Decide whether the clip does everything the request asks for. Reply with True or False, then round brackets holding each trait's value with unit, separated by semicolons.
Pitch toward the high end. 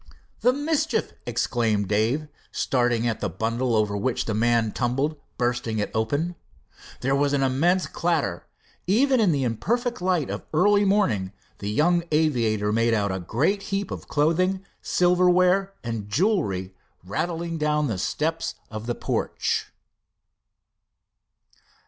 False (140 Hz)